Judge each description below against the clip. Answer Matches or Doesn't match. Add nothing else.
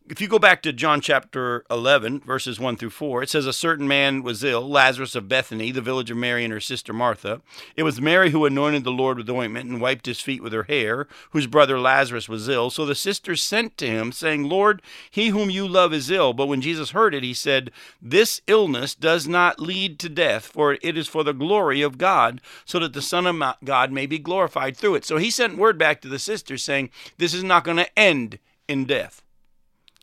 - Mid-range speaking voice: Matches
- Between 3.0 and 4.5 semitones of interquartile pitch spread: Doesn't match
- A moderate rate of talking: Doesn't match